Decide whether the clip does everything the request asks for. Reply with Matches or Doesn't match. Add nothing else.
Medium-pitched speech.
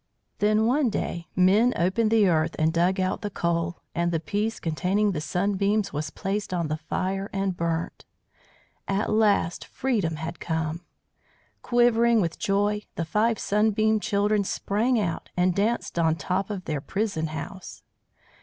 Doesn't match